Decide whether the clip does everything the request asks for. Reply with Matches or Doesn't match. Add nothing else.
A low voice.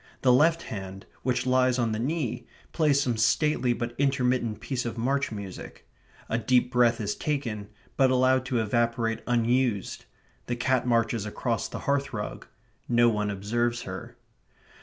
Matches